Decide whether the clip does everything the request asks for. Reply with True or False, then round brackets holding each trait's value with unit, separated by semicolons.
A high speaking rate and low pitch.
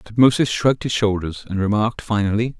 False (160 wpm; 110 Hz)